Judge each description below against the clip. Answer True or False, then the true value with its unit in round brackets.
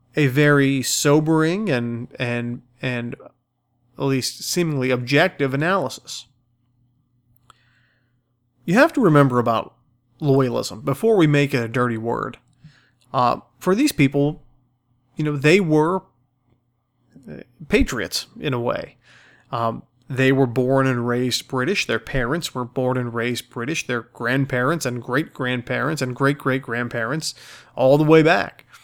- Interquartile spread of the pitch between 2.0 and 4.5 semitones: True (3.0 semitones)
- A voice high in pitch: False (130 Hz)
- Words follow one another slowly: True (130 wpm)